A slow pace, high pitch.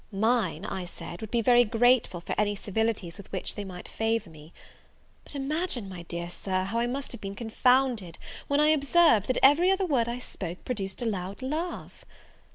No: average, 190 wpm; high, 225 Hz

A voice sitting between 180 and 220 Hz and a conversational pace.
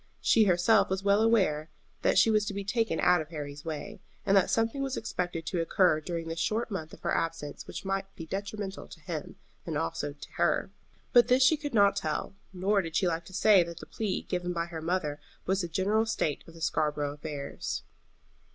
No: medium, 185 Hz; fast, 215 wpm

